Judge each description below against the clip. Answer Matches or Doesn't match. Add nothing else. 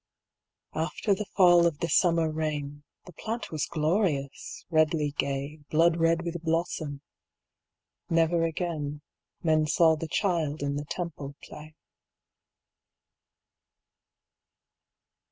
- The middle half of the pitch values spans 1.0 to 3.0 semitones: Matches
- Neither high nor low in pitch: Matches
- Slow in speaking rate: Matches